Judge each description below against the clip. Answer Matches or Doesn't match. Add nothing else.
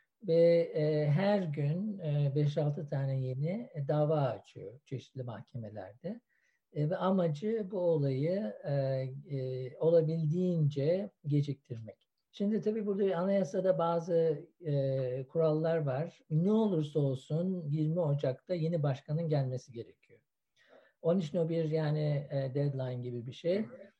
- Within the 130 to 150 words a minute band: Doesn't match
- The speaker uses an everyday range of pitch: Matches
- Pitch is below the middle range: Doesn't match